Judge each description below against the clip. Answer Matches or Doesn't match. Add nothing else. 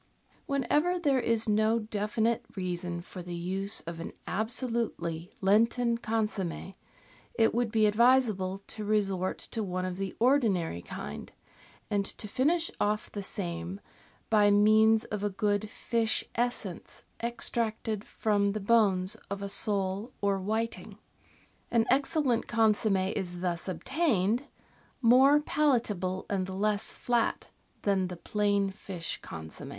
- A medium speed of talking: Doesn't match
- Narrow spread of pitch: Doesn't match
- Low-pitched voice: Doesn't match